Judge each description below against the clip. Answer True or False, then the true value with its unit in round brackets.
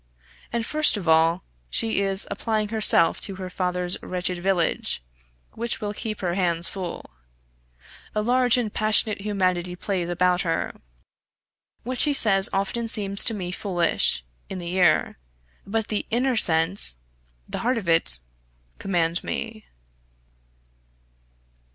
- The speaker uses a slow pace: True (130 wpm)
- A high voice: True (195 Hz)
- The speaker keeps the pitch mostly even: False (3.6 semitones)